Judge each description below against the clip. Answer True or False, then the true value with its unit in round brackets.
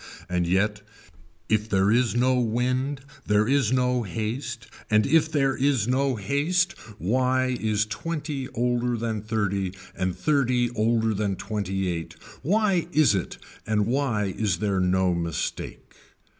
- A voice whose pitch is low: True (115 Hz)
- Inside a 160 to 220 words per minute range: False (140 wpm)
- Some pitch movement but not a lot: True (4.1 semitones)